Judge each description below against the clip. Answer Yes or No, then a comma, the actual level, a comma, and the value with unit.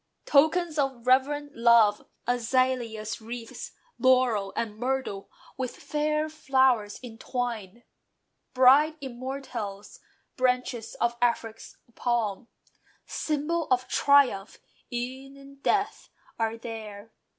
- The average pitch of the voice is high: Yes, very high, 250 Hz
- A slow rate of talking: Yes, slow, 95 wpm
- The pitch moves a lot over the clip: No, average, 3.4 semitones